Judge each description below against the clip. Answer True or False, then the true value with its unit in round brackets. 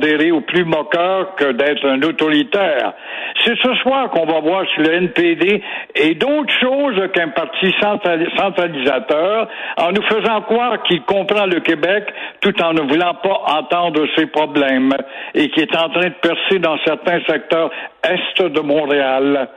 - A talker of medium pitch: True (175 Hz)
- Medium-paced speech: True (155 wpm)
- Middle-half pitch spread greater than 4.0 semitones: True (4.8 semitones)